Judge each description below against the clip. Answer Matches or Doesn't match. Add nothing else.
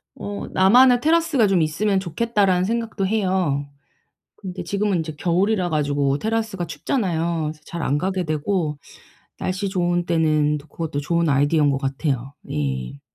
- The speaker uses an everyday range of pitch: Matches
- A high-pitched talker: Doesn't match